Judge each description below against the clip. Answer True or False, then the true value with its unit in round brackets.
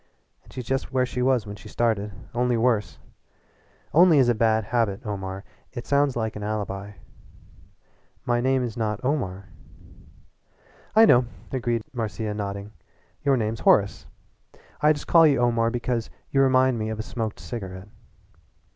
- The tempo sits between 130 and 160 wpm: True (155 wpm)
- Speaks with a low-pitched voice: True (115 Hz)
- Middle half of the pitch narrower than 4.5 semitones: True (3.4 semitones)